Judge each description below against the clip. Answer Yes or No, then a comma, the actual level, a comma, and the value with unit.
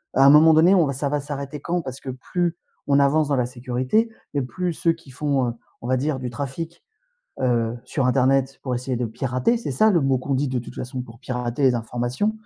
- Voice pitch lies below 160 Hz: Yes, low, 135 Hz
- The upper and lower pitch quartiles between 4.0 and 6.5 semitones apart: No, average, 3.3 semitones